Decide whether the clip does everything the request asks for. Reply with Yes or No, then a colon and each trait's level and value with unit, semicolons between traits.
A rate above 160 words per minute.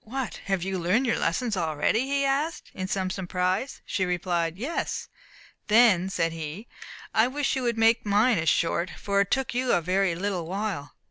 Yes: average, 185 wpm